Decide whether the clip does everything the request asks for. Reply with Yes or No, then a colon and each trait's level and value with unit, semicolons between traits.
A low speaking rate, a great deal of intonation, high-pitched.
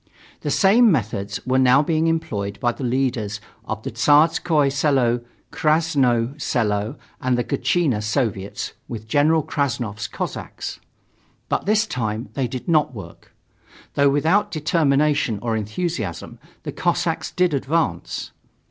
No: slow, 130 wpm; wide, 5.8 semitones; low, 135 Hz